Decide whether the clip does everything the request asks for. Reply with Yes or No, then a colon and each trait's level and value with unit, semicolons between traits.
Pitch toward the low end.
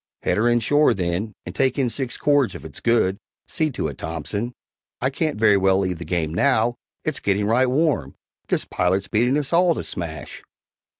Yes: low, 115 Hz